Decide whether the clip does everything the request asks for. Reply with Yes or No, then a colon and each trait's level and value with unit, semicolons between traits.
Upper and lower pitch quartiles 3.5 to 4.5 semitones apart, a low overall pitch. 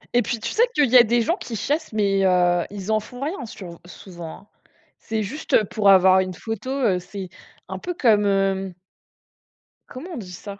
No: average, 4.2 semitones; high, 205 Hz